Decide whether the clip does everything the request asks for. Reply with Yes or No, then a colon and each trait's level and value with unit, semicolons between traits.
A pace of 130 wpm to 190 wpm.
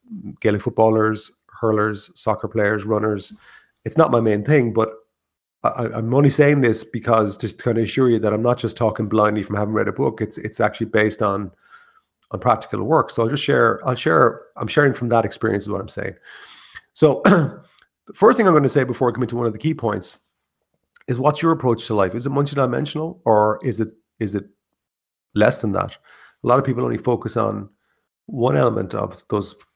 No: average, 200 wpm